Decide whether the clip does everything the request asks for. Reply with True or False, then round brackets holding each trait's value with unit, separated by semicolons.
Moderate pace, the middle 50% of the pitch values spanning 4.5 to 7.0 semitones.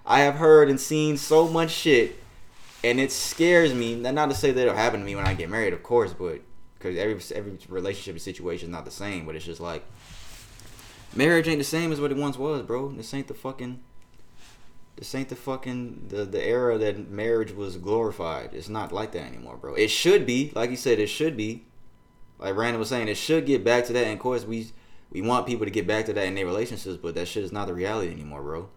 False (240 wpm; 5.4 semitones)